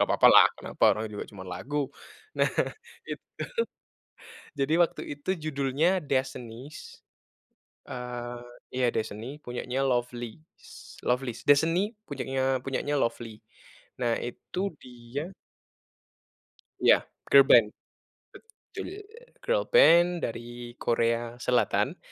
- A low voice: Yes, low, 130 Hz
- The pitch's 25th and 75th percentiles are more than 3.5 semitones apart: Yes, average, 3.9 semitones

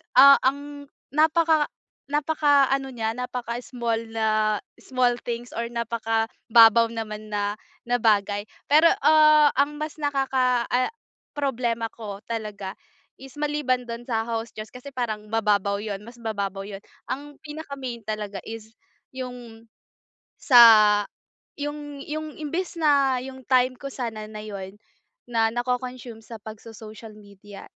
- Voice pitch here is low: No, high, 240 Hz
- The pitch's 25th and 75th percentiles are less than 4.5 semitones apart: Yes, average, 4.0 semitones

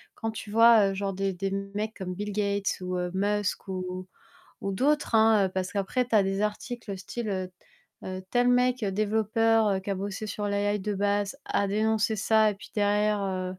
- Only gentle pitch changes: Yes, narrow, 2.1 semitones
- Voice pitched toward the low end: No, high, 205 Hz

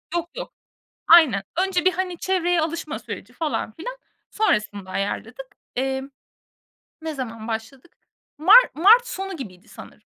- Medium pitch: No, very high, 320 Hz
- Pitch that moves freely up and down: Yes, wide, 8.3 semitones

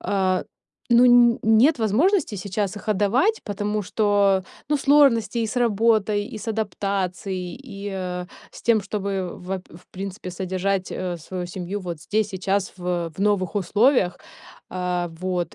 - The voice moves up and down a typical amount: Yes, average, 3.0 semitones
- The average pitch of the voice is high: Yes, high, 200 Hz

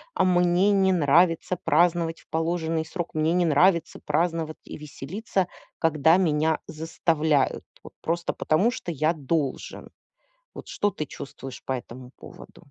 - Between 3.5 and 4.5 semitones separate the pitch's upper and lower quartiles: No, narrow, 2.4 semitones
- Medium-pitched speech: Yes, medium, 165 Hz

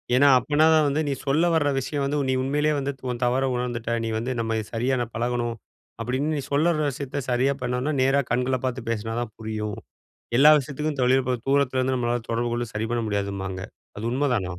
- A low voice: Yes, low, 125 Hz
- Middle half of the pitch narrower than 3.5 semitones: Yes, average, 3.1 semitones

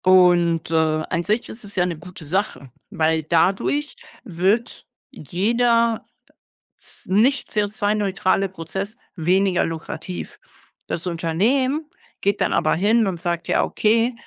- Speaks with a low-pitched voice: No, high, 190 Hz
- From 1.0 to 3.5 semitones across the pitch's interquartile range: No, average, 4.3 semitones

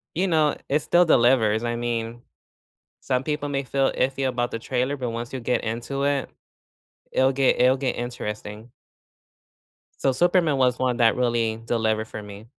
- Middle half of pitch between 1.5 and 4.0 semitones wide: Yes, average, 2.9 semitones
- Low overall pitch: Yes, low, 125 Hz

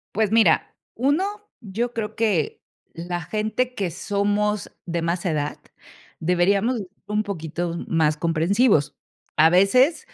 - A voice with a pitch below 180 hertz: No, high, 200 Hz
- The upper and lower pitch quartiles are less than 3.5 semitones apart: No, average, 4.6 semitones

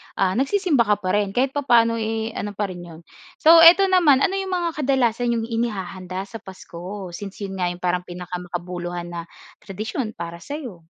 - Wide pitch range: Yes, wide, 5.9 semitones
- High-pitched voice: Yes, high, 205 Hz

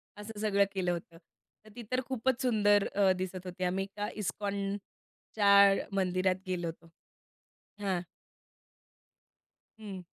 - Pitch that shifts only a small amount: Yes, narrow, 2.1 semitones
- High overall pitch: Yes, high, 200 Hz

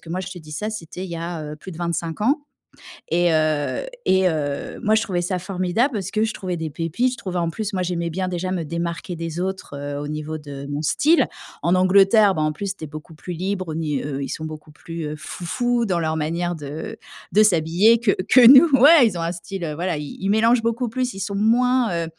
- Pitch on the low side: No, medium, 175 Hz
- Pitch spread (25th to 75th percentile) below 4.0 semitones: No, average, 4.8 semitones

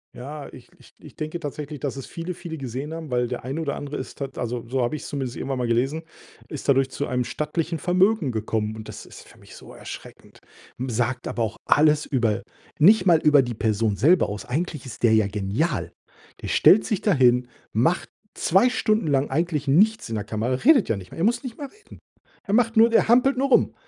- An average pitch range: No, wide, 6.1 semitones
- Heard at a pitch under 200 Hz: Yes, medium, 140 Hz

